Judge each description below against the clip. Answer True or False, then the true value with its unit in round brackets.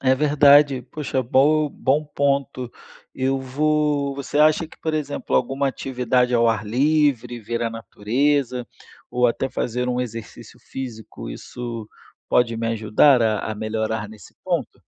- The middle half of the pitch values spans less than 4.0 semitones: True (3.5 semitones)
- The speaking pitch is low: True (130 Hz)